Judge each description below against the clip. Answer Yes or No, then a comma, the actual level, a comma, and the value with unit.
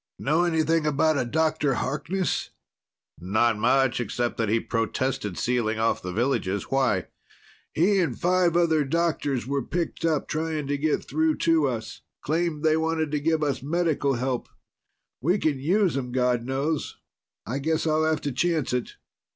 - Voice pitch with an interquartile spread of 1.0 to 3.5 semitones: No, average, 4.5 semitones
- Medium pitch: Yes, medium, 145 Hz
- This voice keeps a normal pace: Yes, average, 160 wpm